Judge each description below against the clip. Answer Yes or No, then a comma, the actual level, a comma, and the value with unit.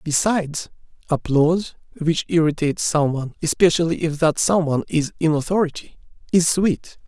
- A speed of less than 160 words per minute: Yes, slow, 135 wpm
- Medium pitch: Yes, medium, 160 Hz